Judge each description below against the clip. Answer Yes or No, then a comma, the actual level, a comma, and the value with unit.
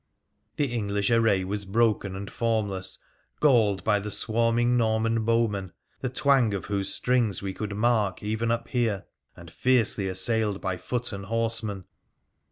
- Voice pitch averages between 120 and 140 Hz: No, low, 110 Hz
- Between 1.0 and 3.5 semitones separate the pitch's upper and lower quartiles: Yes, average, 2.8 semitones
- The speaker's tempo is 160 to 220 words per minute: No, average, 150 wpm